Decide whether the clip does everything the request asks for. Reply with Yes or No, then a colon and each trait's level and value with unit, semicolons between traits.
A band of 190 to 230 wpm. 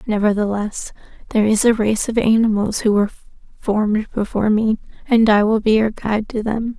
No: average, 175 wpm